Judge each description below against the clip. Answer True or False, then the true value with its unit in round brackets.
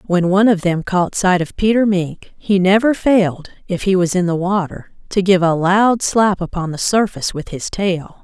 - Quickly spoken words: False (195 wpm)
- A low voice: False (185 Hz)